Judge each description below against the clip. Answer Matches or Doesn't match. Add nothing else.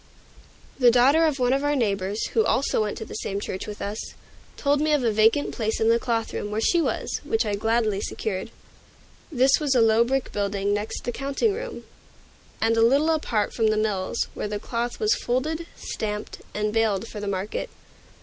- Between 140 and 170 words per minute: Doesn't match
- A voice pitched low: Doesn't match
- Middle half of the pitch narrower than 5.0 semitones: Matches